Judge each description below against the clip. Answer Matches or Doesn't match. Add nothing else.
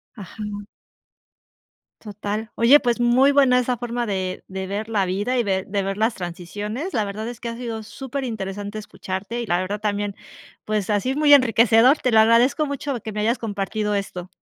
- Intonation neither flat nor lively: Matches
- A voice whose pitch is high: Matches